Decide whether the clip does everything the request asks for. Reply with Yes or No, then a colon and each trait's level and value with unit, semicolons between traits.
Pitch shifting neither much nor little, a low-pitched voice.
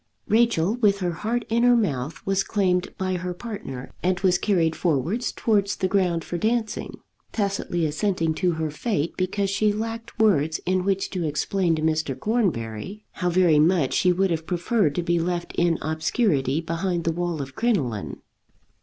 No: average, 4.1 semitones; medium, 180 Hz